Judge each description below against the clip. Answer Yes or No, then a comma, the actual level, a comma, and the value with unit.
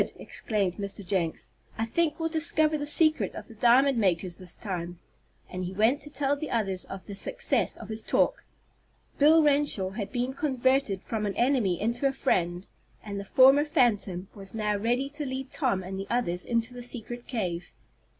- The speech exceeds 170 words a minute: Yes, average, 185 wpm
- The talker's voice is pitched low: No, high, 230 Hz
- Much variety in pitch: Yes, wide, 6.0 semitones